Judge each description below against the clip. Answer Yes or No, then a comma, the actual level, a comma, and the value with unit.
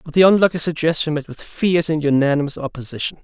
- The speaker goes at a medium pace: Yes, average, 185 wpm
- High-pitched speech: No, medium, 155 Hz